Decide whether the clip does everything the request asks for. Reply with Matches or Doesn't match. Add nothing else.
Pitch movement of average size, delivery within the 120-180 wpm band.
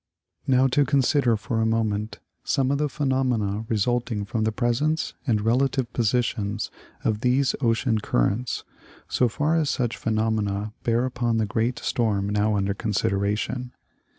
Matches